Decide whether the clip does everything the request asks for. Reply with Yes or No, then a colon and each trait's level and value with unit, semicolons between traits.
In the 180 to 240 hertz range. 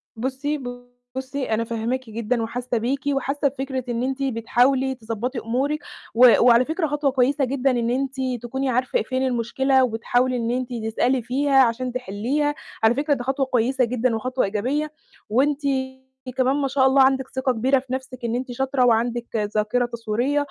No: very high, 255 Hz